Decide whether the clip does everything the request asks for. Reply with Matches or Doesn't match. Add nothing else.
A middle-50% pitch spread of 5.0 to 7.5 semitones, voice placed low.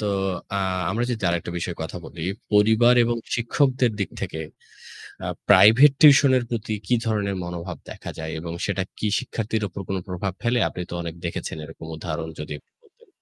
Matches